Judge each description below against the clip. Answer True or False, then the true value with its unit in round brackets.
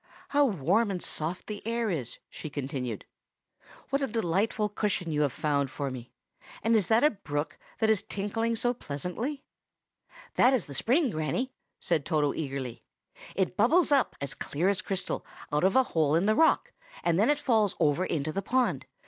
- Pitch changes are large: True (7.4 semitones)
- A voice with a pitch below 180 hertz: False (190 Hz)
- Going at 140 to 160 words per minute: False (180 wpm)